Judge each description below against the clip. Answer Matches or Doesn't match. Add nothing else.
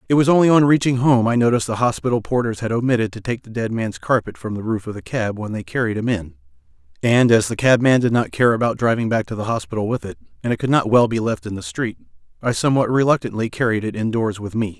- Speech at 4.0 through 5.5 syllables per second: Doesn't match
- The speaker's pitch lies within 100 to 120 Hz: Matches